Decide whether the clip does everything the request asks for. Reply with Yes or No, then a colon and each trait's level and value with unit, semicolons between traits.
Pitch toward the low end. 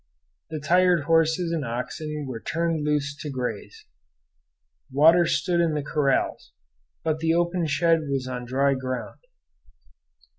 No: medium, 150 Hz